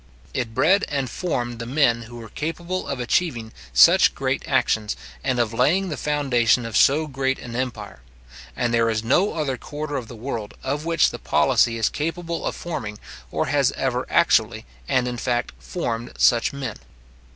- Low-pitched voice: Yes, low, 125 Hz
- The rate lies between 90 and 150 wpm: No, average, 175 wpm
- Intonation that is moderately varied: Yes, average, 4.3 semitones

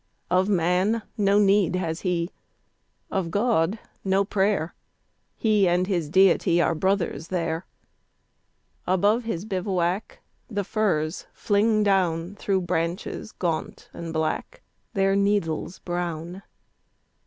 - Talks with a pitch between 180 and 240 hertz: Yes, medium, 185 Hz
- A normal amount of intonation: Yes, average, 3.0 semitones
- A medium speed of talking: No, slow, 110 wpm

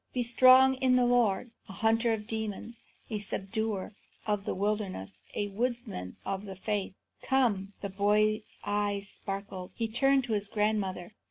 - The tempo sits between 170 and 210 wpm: No, average, 160 wpm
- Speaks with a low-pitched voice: No, high, 210 Hz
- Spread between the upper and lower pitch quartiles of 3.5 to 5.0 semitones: No, average, 2.8 semitones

